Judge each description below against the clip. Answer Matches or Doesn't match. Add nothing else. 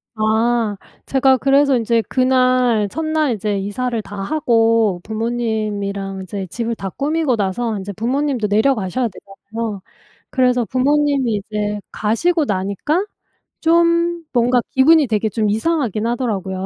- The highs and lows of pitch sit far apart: Doesn't match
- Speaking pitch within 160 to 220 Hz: Doesn't match